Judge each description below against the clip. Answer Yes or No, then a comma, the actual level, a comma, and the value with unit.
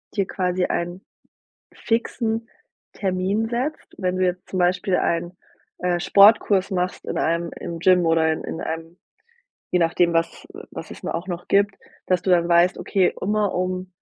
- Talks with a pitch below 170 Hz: No, medium, 180 Hz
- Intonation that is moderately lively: No, narrow, 2.2 semitones